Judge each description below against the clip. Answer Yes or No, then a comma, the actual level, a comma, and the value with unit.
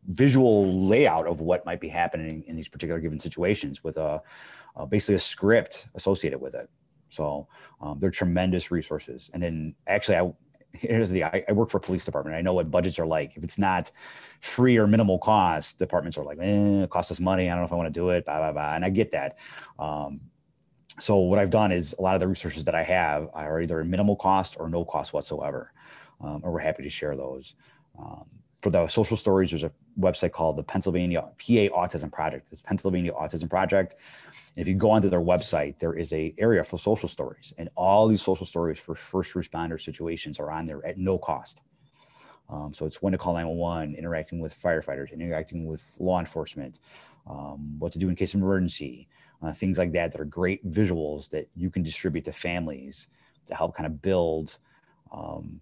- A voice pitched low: Yes, very low, 85 Hz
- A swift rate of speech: Yes, fast, 210 wpm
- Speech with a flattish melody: No, average, 3.1 semitones